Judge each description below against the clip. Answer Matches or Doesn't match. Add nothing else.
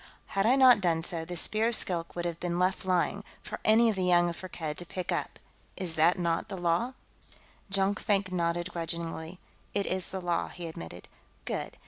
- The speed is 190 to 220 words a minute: Matches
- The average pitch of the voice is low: Doesn't match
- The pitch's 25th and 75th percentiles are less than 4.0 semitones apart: Matches